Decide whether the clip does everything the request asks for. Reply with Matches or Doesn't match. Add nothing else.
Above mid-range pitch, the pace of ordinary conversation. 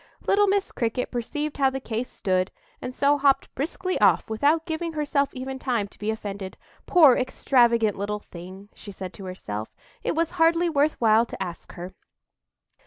Matches